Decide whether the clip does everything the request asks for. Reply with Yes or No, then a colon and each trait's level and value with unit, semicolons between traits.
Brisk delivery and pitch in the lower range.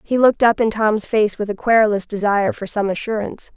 No: fast, 220 wpm; high, 215 Hz